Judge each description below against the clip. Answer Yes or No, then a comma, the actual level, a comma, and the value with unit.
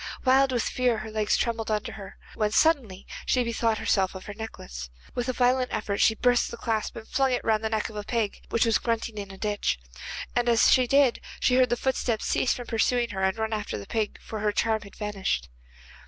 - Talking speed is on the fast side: Yes, fast, 230 wpm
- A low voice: No, high, 225 Hz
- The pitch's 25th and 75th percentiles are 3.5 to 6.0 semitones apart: No, average, 2.7 semitones